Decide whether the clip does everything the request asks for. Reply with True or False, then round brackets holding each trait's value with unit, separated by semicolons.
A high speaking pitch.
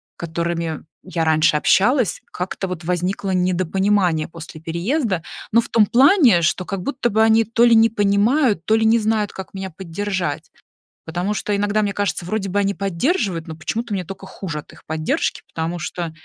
True (195 Hz)